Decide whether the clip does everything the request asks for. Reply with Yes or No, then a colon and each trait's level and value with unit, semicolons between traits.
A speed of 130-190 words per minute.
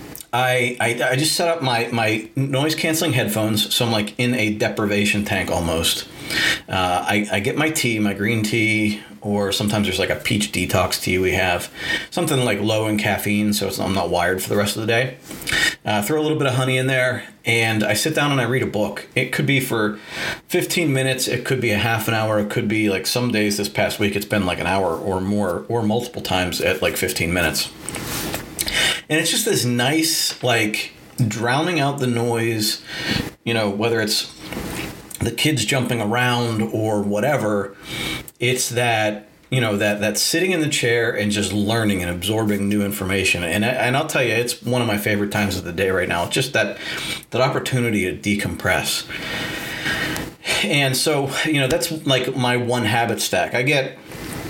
No: average, 200 wpm